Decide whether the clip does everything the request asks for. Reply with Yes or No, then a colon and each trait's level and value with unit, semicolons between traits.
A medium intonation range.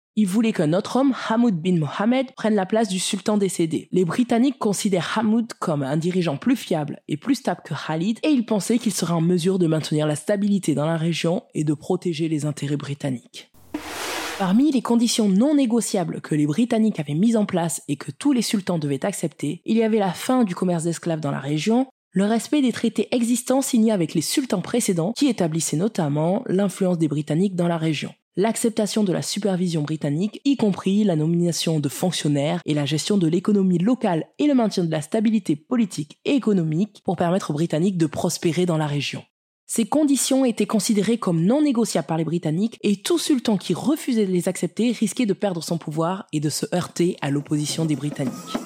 No: wide, 5.7 semitones